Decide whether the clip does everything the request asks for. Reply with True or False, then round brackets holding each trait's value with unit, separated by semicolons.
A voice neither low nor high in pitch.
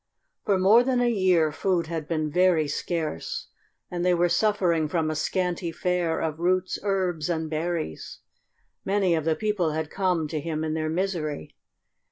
True (170 Hz)